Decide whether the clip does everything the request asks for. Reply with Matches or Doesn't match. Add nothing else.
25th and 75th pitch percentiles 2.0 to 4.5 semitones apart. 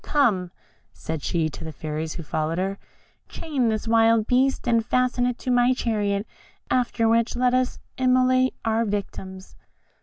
Doesn't match